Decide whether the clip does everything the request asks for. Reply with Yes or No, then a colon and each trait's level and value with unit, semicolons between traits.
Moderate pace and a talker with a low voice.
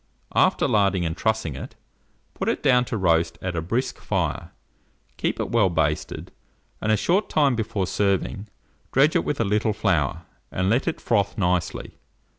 Yes: average, 170 wpm; low, 100 Hz